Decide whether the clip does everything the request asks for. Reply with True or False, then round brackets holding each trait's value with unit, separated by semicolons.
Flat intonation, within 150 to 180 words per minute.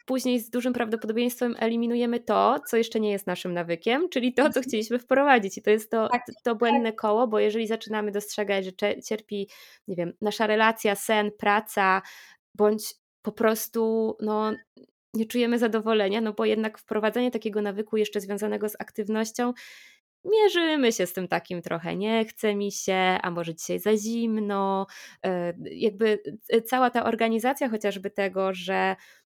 True (2.3 semitones; 155 wpm)